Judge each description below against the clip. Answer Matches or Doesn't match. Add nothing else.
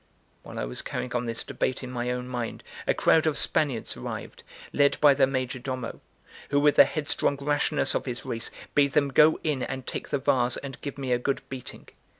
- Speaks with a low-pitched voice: Matches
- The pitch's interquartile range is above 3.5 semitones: Doesn't match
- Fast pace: Matches